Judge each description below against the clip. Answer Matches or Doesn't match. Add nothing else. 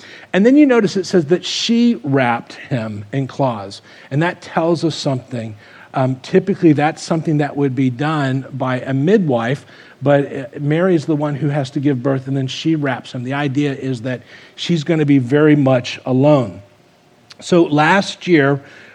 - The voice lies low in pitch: Doesn't match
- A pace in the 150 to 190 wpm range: Matches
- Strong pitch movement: Doesn't match